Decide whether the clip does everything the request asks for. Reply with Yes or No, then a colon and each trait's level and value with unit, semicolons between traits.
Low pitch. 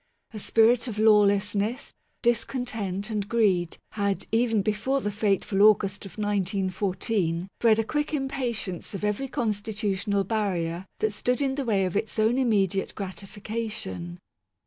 No: high, 210 Hz